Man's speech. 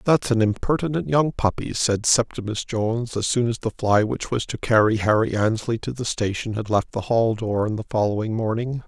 Yes: male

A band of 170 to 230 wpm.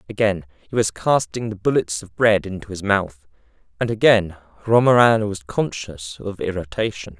No: average, 150 wpm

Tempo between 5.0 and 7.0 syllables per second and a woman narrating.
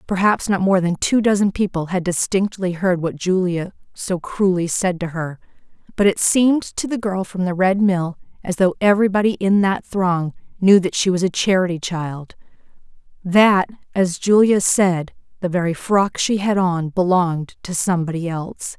No: 4.8 syllables/s; female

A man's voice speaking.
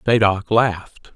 Yes: male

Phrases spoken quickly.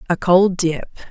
No: average, 165 wpm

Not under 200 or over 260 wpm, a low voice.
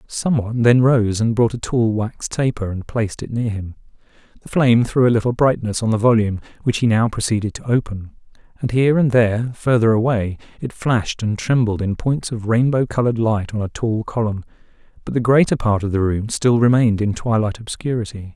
Yes: fast, 205 wpm; low, 115 Hz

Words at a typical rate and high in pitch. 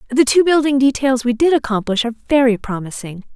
Yes: average, 180 wpm; very high, 255 Hz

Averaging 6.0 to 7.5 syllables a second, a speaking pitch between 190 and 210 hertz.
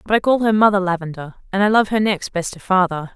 Yes: 6.3 syllables/s; high, 195 Hz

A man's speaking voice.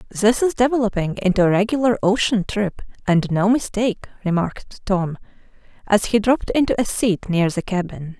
No: female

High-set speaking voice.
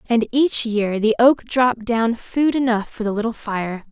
Yes: high, 230 Hz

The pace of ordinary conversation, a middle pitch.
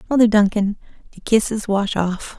No: average, 150 wpm; high, 210 Hz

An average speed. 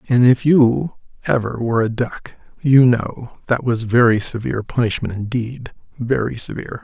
Yes: average, 150 wpm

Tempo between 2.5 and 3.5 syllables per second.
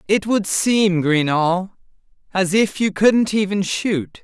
Yes: 3.4 syllables/s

